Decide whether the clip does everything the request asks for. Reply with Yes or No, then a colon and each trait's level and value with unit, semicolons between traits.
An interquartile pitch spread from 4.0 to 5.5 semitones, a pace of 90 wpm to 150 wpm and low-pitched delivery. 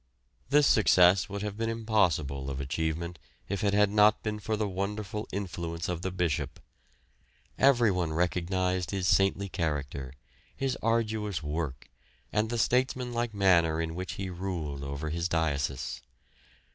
Yes: average, 4.5 semitones; average, 140 wpm; very low, 95 Hz